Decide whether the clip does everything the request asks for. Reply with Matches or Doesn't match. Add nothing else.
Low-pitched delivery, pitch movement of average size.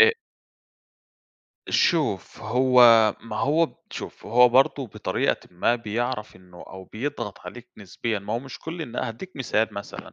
Matches